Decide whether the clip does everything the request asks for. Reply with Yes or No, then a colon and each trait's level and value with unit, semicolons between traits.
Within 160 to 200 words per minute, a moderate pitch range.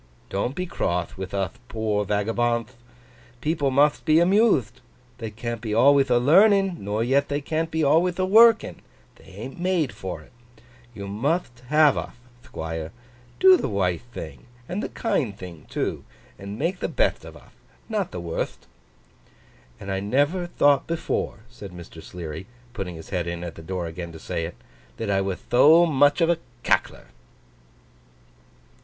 No: average, 165 wpm; wide, 8.8 semitones